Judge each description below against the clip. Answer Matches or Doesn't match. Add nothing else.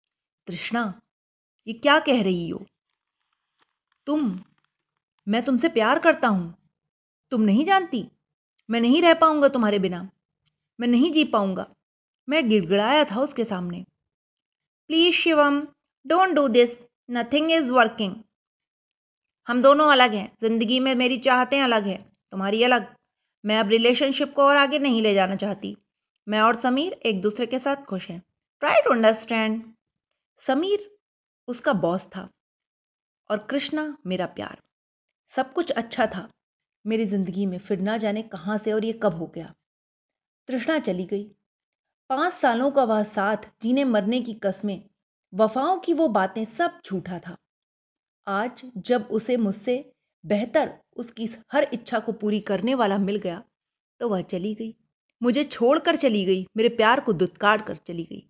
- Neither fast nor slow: Matches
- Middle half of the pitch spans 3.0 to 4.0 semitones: Doesn't match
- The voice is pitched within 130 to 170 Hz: Doesn't match